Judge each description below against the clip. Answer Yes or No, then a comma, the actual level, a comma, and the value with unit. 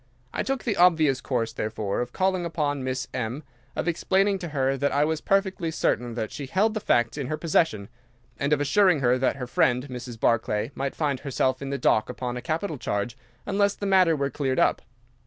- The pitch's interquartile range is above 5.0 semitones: Yes, wide, 5.6 semitones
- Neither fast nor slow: No, fast, 210 wpm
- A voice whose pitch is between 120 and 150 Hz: Yes, medium, 140 Hz